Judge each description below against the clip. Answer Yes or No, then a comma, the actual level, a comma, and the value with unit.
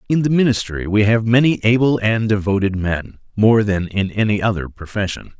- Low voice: Yes, low, 105 Hz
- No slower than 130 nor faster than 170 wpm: Yes, average, 165 wpm